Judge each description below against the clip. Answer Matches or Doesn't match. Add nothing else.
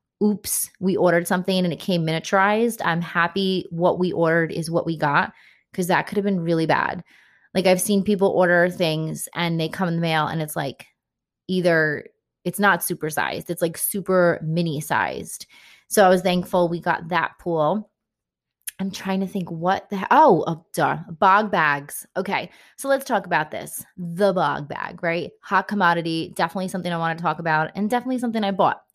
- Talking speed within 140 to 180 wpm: Doesn't match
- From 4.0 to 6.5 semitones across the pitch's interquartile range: Doesn't match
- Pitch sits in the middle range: Matches